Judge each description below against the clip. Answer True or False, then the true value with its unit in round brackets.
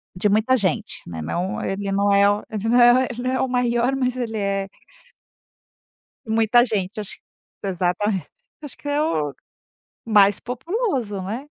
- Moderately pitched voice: False (220 Hz)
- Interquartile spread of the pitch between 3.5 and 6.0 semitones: True (4.0 semitones)